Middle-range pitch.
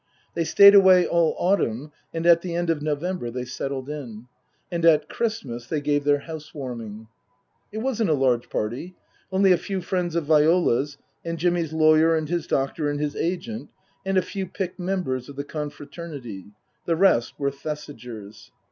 Yes: medium, 155 Hz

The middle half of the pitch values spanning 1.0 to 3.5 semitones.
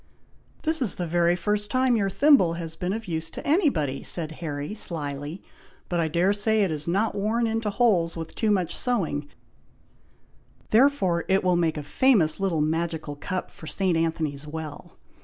No: average, 4.8 semitones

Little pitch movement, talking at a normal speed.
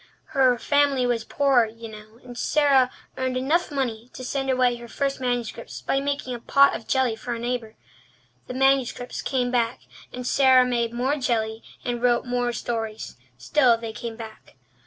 Yes: narrow, 2.3 semitones; average, 175 wpm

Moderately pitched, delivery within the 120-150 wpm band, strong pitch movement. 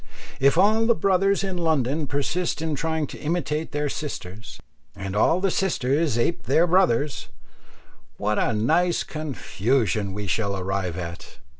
Yes: medium, 150 Hz; average, 145 wpm; wide, 8.0 semitones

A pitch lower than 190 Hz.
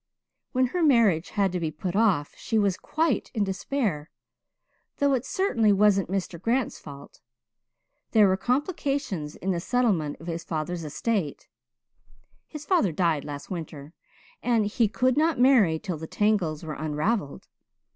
No: high, 195 Hz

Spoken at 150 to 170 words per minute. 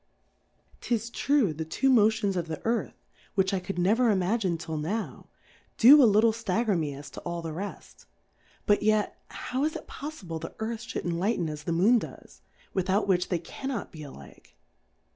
No: average, 185 wpm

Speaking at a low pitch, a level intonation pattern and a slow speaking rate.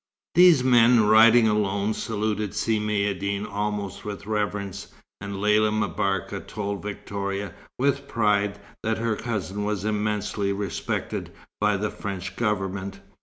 Yes: low, 105 Hz; narrow, 1.4 semitones; slow, 120 wpm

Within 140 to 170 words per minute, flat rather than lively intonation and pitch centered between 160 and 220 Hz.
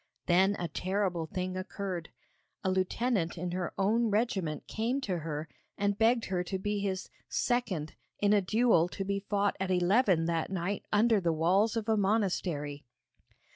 No: average, 165 wpm; average, 3.1 semitones; high, 190 Hz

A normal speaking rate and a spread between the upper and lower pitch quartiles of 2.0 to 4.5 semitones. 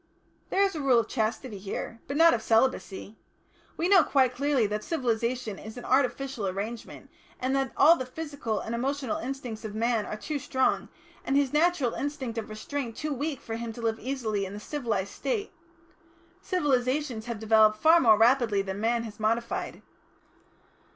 Yes: average, 175 wpm; average, 4.1 semitones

